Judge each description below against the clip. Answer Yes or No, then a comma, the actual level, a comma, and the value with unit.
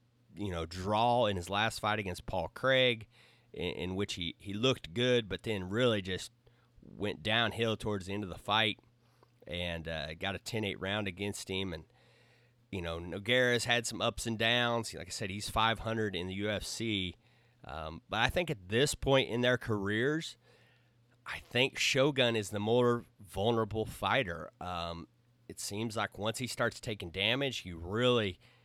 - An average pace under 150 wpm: No, average, 175 wpm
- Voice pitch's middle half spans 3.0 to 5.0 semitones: Yes, average, 3.5 semitones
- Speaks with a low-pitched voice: Yes, low, 110 Hz